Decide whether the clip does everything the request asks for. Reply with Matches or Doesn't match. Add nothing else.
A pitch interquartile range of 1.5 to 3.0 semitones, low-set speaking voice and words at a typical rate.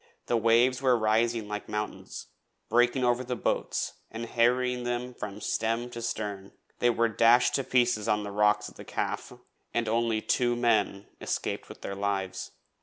Matches